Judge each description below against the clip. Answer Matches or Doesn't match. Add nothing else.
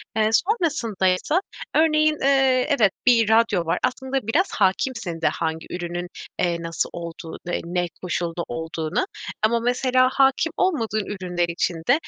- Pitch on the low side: Doesn't match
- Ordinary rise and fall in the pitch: Doesn't match